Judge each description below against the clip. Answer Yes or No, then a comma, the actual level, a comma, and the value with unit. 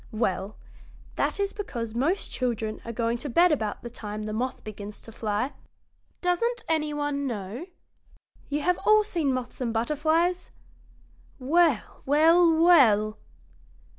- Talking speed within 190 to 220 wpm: No, slow, 135 wpm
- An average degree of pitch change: No, wide, 6.9 semitones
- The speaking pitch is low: No, very high, 265 Hz